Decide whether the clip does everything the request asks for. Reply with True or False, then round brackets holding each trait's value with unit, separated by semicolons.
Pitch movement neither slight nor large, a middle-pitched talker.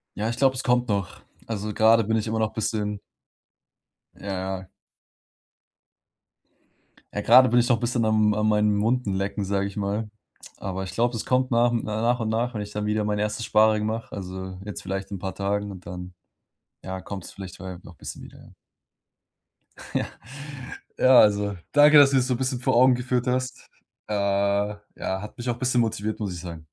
False (3.2 semitones; 105 Hz)